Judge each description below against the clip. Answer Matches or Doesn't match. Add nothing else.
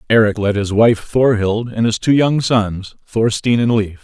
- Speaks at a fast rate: Doesn't match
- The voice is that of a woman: Doesn't match